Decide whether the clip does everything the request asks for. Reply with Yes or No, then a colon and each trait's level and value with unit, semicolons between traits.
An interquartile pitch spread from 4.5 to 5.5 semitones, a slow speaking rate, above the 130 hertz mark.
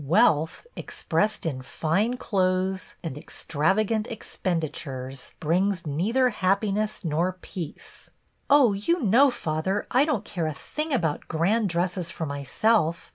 Yes: average, 5.2 semitones; slow, 130 wpm; medium, 185 Hz